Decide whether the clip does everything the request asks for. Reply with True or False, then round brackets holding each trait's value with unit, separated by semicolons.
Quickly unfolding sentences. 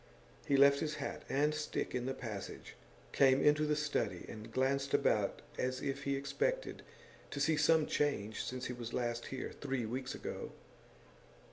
False (165 wpm)